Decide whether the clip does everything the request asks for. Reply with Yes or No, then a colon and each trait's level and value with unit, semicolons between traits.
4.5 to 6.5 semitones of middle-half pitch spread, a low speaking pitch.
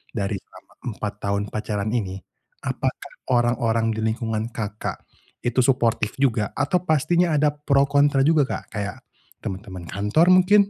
Yes: average, 5.3 semitones; low, 120 Hz